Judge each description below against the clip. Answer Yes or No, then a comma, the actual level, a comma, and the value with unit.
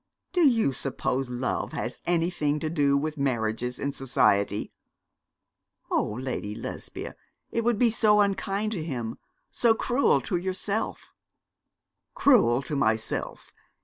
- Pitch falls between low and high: Yes, medium, 150 Hz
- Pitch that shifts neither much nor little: No, wide, 8.8 semitones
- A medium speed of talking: No, slow, 125 wpm